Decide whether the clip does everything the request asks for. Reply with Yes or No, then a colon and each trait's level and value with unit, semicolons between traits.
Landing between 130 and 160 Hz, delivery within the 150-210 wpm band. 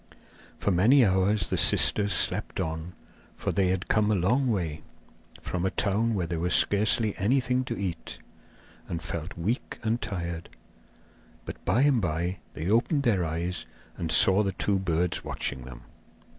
No: very low, 95 Hz; average, 160 wpm